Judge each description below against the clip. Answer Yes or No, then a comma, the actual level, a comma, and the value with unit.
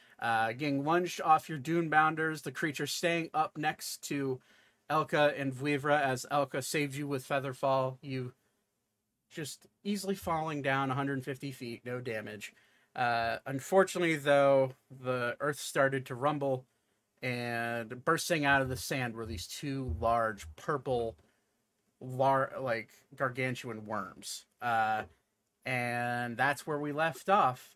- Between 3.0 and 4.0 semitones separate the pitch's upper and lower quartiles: Yes, average, 3.5 semitones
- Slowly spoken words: Yes, slow, 130 wpm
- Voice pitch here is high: No, low, 135 Hz